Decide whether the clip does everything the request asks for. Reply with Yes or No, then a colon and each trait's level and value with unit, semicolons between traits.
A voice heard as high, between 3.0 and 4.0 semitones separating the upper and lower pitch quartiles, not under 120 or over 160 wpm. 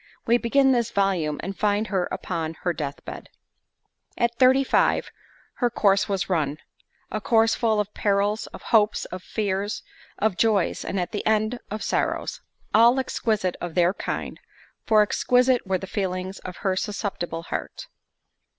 Yes: high, 205 Hz; average, 3.4 semitones; average, 155 wpm